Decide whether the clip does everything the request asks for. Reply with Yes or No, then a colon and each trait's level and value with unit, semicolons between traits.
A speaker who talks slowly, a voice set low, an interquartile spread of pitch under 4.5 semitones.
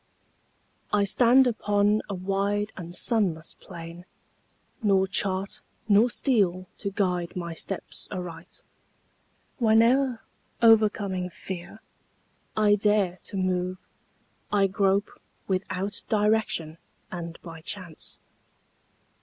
No: slow, 95 wpm; high, 195 Hz; average, 2.7 semitones